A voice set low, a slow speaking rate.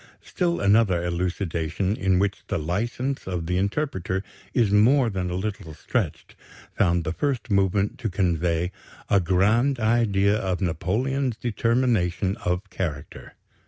Yes: low, 100 Hz; slow, 130 wpm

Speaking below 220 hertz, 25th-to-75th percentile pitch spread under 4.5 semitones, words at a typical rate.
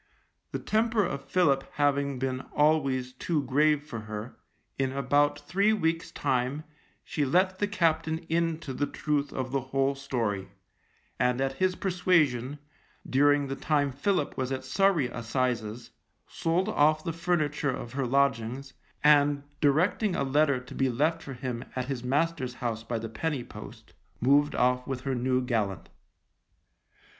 Yes: medium, 140 Hz; average, 3.4 semitones; average, 150 wpm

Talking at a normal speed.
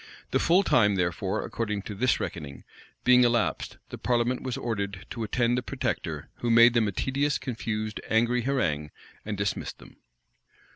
Yes: average, 160 wpm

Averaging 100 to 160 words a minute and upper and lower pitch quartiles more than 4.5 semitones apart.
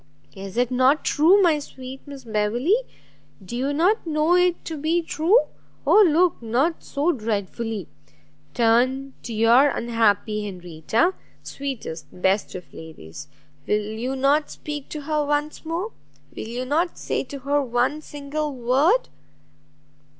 Yes: average, 140 wpm; average, 5.3 semitones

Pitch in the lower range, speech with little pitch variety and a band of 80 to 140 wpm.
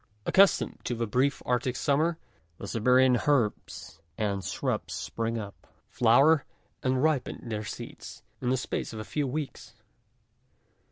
No: low, 125 Hz; average, 3.7 semitones; slow, 135 wpm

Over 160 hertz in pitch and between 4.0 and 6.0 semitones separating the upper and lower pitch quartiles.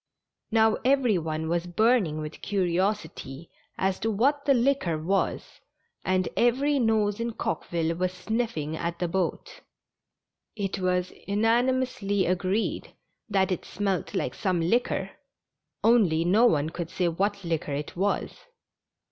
Yes: high, 190 Hz; average, 4.7 semitones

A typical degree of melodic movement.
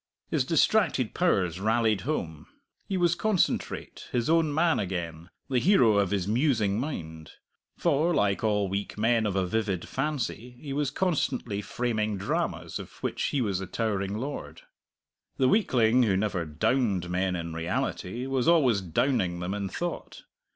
No: wide, 6.2 semitones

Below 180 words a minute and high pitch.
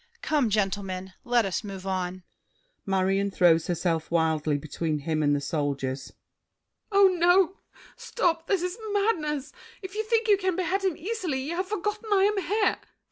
Yes: average, 160 wpm; very high, 265 Hz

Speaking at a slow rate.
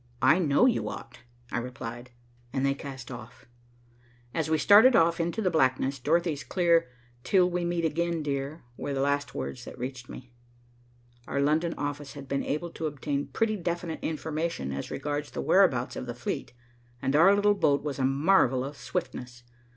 No: average, 175 wpm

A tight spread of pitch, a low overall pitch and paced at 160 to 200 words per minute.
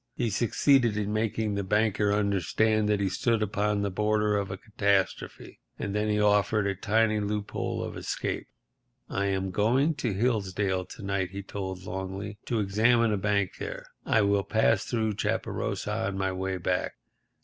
Yes: narrow, 1.8 semitones; low, 105 Hz; average, 170 wpm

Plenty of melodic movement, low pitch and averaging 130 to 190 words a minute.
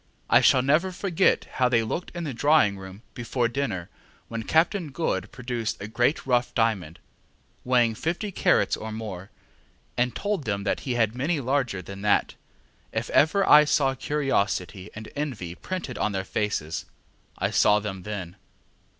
Yes: wide, 5.9 semitones; low, 120 Hz; average, 160 wpm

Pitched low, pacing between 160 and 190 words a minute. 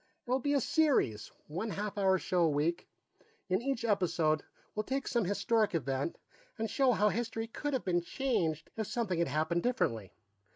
No: high, 205 Hz; average, 175 wpm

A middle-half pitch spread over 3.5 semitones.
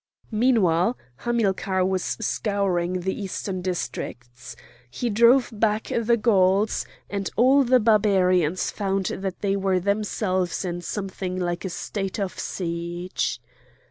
No: average, 2.9 semitones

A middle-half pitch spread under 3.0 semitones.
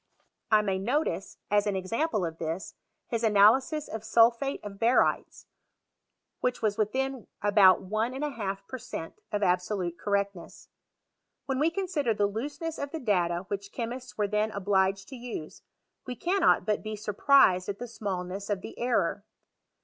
No: average, 4.3 semitones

